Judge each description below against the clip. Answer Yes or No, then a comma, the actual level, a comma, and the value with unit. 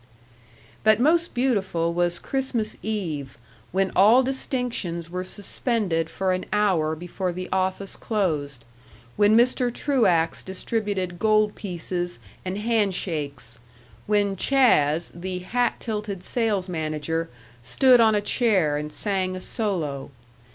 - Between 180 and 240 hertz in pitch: Yes, high, 190 Hz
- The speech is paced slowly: Yes, slow, 120 wpm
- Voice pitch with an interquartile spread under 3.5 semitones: No, average, 4.3 semitones